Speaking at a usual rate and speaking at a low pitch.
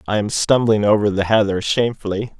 Yes: average, 175 wpm; low, 105 Hz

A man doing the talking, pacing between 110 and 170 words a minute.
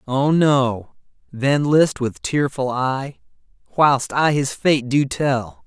Yes: male; average, 140 wpm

